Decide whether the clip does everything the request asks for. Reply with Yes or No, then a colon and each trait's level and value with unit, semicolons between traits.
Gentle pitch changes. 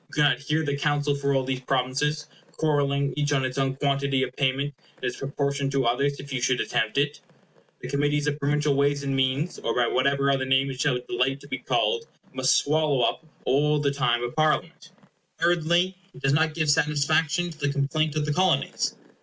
Yes: narrow, 1.8 semitones